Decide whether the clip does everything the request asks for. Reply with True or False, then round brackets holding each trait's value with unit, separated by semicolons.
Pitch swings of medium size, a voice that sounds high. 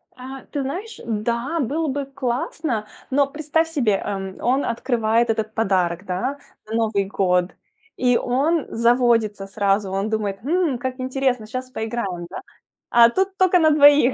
True (4.6 semitones; 240 Hz)